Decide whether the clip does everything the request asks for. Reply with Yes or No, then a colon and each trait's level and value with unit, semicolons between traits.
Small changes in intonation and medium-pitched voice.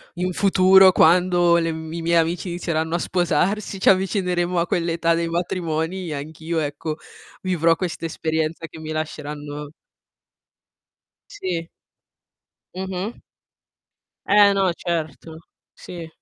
Yes: narrow, 2.2 semitones; medium, 170 Hz